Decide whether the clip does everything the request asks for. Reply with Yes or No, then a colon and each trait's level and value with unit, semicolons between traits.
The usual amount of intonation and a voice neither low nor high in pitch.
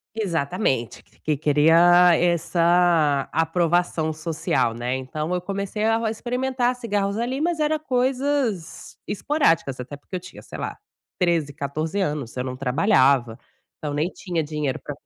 No: wide, 6.3 semitones; medium, 170 Hz